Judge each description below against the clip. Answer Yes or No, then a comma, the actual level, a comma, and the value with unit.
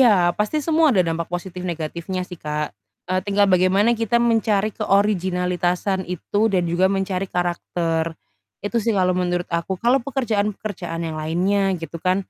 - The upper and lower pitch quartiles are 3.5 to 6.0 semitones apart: No, average, 2.8 semitones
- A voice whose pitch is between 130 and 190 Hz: Yes, medium, 185 Hz